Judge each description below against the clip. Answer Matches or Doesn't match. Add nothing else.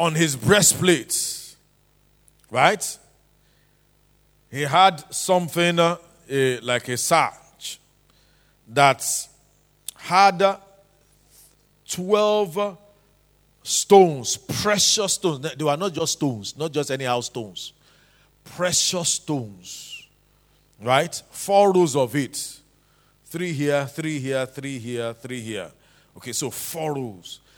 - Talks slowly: Matches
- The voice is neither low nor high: Matches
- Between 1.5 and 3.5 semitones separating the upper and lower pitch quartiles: Doesn't match